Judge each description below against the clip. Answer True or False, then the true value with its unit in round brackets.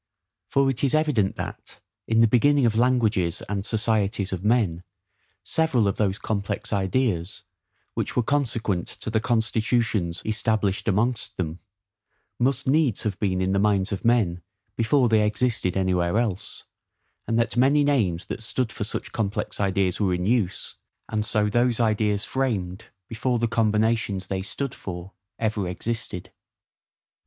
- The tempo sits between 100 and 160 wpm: True (150 wpm)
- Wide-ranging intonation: False (3.6 semitones)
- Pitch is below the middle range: True (110 Hz)